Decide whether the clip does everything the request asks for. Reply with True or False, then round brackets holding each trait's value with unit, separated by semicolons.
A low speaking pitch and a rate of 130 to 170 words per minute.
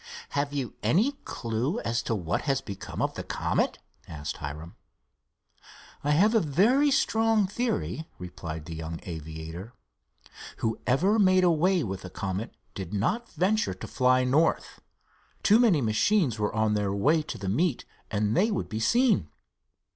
True (125 Hz; 150 wpm)